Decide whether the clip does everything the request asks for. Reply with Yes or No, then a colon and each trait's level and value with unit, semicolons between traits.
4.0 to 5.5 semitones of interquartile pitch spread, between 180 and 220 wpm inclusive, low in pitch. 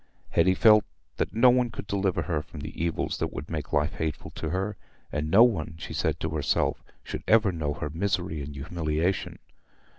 Yes: average, 4.6 semitones; average, 190 wpm; very low, 85 Hz